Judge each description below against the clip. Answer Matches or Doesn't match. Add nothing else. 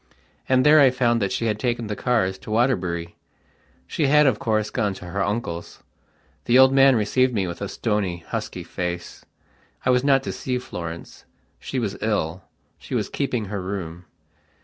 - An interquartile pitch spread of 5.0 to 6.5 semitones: Matches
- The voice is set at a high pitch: Doesn't match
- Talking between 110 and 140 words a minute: Doesn't match